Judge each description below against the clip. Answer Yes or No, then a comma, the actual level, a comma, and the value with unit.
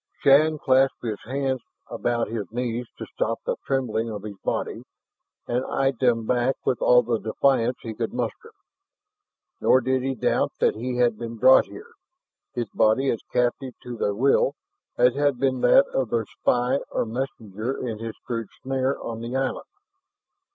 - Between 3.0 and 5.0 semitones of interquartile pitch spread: No, narrow, 2.6 semitones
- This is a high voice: No, low, 125 Hz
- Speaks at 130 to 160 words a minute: No, average, 170 wpm